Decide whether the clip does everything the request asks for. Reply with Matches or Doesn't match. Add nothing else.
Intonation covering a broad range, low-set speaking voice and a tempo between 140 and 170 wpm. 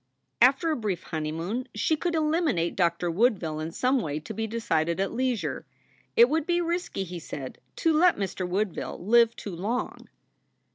Doesn't match